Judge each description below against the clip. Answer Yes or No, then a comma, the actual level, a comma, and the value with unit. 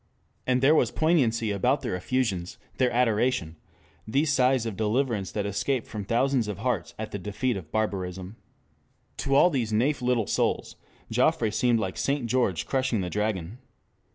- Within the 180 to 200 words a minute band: No, average, 160 wpm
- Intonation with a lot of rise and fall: No, average, 4.1 semitones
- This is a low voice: Yes, low, 115 Hz